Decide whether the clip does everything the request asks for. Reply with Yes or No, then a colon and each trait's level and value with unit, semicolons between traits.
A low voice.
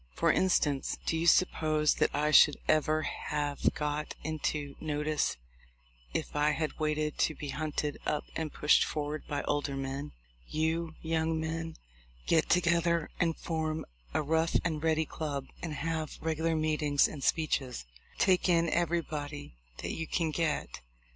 No: medium, 155 Hz